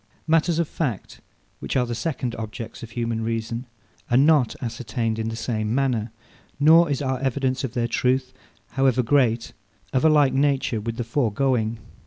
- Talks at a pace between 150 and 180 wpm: Yes, average, 170 wpm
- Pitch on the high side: No, low, 125 Hz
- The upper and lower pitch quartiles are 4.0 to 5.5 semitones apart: No, average, 3.2 semitones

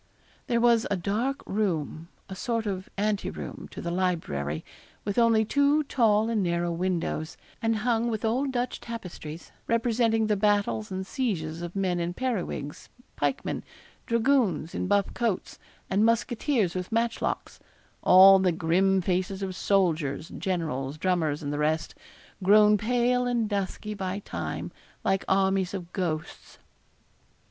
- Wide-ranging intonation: No, average, 4.7 semitones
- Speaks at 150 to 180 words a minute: No, average, 140 wpm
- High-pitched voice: Yes, high, 195 Hz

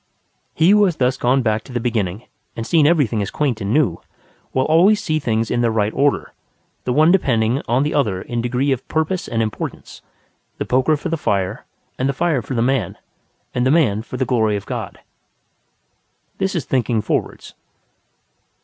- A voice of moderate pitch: No, low, 125 Hz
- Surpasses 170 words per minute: Yes, average, 190 wpm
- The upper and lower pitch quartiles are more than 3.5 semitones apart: Yes, average, 5.2 semitones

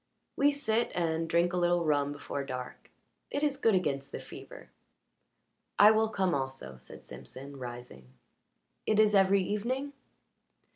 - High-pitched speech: No, medium, 175 Hz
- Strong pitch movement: Yes, wide, 7.8 semitones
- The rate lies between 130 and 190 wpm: Yes, average, 145 wpm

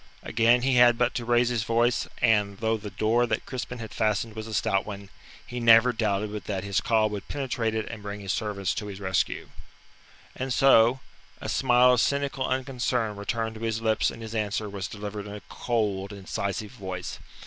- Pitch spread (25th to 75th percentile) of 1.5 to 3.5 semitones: Yes, average, 2.9 semitones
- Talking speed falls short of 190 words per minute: No, average, 200 wpm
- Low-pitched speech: Yes, low, 110 Hz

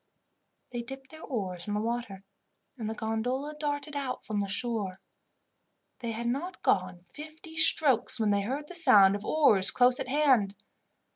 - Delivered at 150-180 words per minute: Yes, average, 165 wpm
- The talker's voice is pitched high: Yes, high, 240 Hz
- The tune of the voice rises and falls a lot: Yes, wide, 5.9 semitones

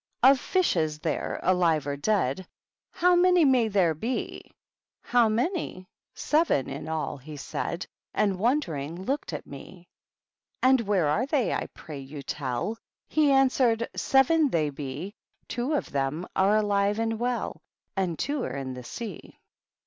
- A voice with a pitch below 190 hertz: No, high, 200 Hz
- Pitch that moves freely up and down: Yes, wide, 8.8 semitones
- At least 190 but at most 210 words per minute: No, average, 165 wpm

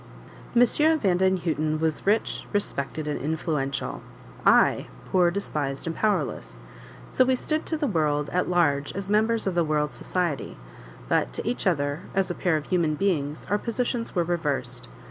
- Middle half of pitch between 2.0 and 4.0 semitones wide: No, average, 5.2 semitones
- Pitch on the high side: No, medium, 175 Hz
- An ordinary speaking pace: Yes, average, 160 wpm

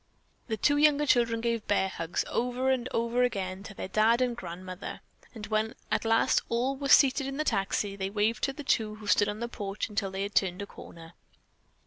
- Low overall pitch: No, high, 220 Hz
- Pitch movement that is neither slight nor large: Yes, average, 4.0 semitones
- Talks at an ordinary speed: No, fast, 210 wpm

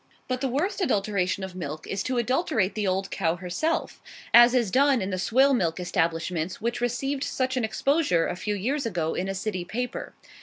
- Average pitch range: No, wide, 6.0 semitones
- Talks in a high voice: Yes, high, 215 Hz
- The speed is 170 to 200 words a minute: Yes, average, 195 wpm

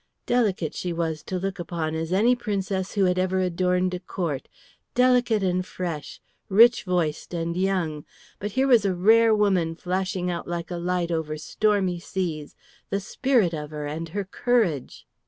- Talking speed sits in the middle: Yes, average, 170 wpm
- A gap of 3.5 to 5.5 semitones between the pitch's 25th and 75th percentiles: No, average, 3.1 semitones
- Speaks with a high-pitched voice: No, medium, 180 Hz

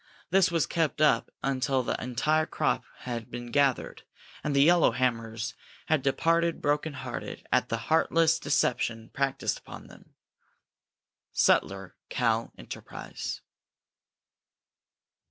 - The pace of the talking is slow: Yes, slow, 110 wpm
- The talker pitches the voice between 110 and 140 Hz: Yes, low, 135 Hz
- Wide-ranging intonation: No, average, 4.6 semitones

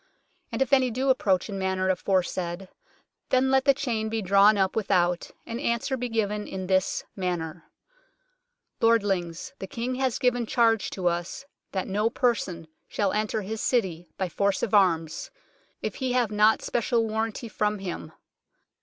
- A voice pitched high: Yes, high, 210 Hz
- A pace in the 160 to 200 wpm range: Yes, average, 165 wpm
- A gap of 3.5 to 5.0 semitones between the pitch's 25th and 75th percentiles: Yes, average, 4.2 semitones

